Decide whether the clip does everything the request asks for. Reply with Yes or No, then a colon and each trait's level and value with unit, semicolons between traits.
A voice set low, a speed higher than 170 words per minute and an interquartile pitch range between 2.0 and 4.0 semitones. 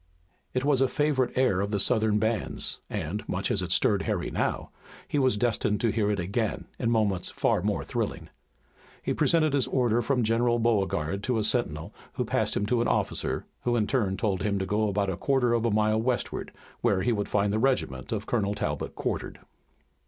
Yes: low, 110 Hz; fast, 205 wpm; average, 3.3 semitones